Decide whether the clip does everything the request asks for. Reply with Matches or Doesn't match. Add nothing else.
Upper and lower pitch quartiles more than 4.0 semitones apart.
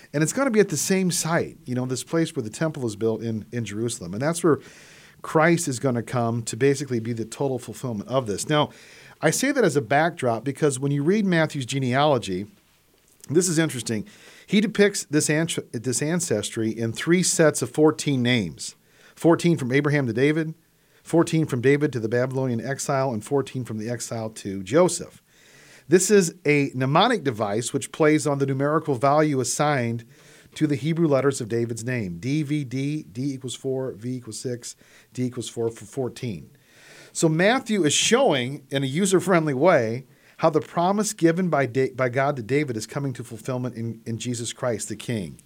Matches